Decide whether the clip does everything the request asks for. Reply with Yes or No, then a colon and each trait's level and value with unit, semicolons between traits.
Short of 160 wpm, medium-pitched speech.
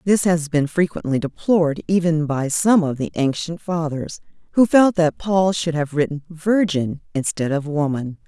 No: average, 165 wpm; medium, 160 Hz